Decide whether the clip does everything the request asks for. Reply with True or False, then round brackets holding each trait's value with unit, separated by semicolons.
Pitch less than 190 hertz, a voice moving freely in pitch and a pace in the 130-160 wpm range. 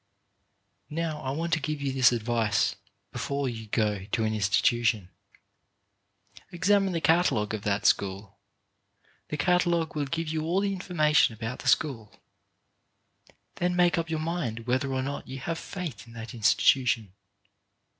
True (135 Hz; 6.7 semitones; 150 wpm)